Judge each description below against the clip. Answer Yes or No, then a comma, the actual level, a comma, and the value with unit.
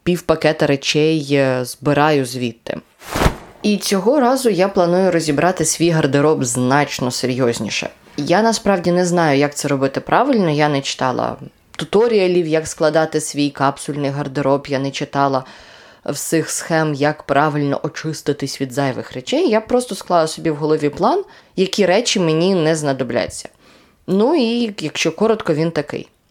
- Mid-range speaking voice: Yes, medium, 155 Hz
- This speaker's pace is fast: No, average, 135 wpm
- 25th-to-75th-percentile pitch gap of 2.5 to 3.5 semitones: No, average, 4.2 semitones